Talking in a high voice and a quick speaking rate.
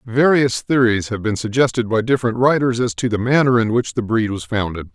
No: low, 120 Hz; fast, 220 wpm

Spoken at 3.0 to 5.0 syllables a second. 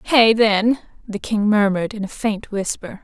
Yes: 4.5 syllables/s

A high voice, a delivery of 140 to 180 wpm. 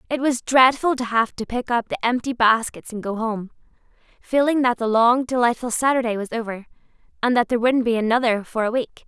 No: high, 235 Hz; fast, 205 wpm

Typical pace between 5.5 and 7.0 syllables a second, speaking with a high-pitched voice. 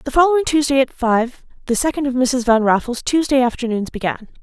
Yes: 5.7 syllables/s; very high, 255 Hz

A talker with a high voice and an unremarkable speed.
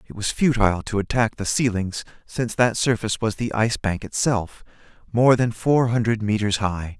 No: low, 110 Hz; average, 180 wpm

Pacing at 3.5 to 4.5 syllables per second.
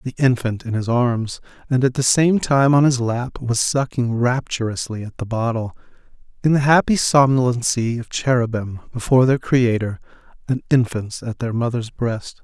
No: 4.8 syllables/s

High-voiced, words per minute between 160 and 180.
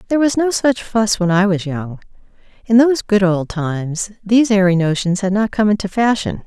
No: high, 205 Hz; fast, 205 wpm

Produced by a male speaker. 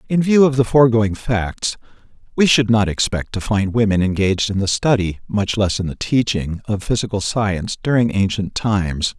Yes: male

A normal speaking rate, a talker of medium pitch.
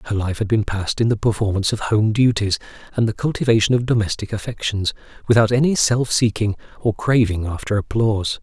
No: average, 180 wpm; low, 110 Hz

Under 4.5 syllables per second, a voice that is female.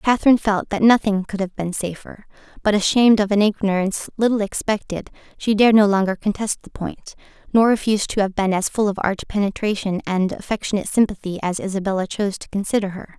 No: 6.3 syllables/s; female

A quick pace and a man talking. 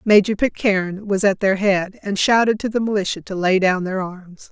No: fast, 210 wpm; female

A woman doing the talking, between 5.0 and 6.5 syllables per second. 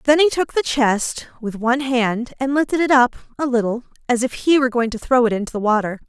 Yes: female; 5.9 syllables/s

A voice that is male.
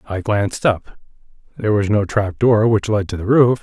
Yes: male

